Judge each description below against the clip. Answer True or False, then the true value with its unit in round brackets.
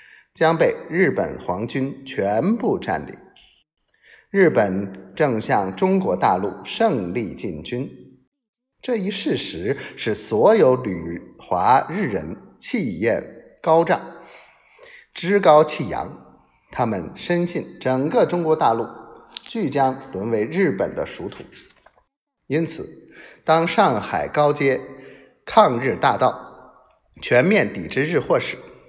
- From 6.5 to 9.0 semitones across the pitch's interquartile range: True (7.5 semitones)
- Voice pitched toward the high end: False (160 Hz)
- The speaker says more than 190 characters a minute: False (160 characters per minute)